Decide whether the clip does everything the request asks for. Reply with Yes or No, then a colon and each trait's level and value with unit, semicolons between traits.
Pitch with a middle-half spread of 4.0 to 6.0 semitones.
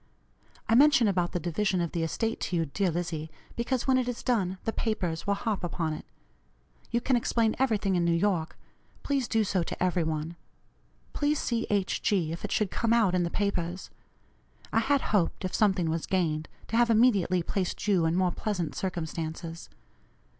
Yes: average, 4.8 semitones